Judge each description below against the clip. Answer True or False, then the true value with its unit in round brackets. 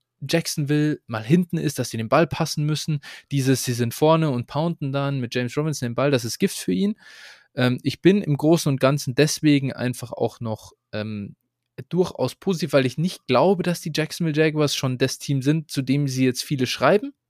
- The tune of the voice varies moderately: True (4.2 semitones)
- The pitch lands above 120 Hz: True (140 Hz)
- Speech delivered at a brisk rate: True (205 wpm)